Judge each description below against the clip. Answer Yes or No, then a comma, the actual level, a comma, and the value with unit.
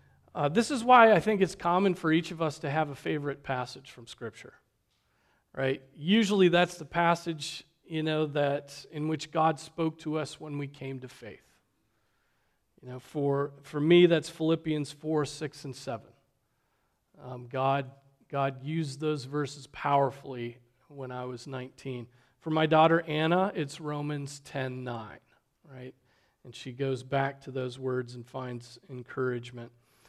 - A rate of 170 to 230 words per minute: No, average, 160 wpm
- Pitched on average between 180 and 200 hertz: No, medium, 140 Hz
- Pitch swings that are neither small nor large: Yes, average, 3.5 semitones